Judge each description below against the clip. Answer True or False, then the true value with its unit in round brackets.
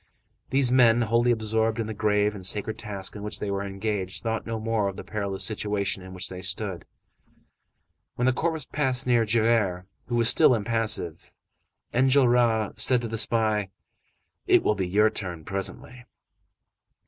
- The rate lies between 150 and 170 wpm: True (165 wpm)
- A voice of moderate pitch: False (110 Hz)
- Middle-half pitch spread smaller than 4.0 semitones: True (2.9 semitones)